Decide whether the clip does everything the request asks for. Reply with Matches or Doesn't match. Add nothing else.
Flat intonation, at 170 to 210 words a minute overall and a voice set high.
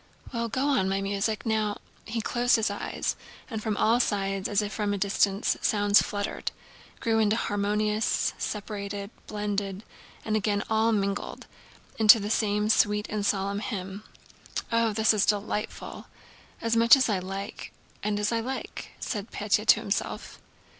Doesn't match